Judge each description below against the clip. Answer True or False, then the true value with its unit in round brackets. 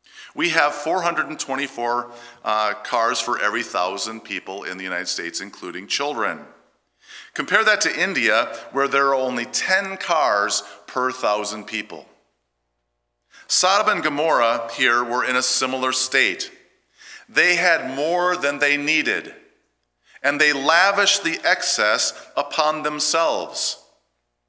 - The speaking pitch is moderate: False (125 Hz)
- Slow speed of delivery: True (125 wpm)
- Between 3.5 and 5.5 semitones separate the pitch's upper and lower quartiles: True (5.2 semitones)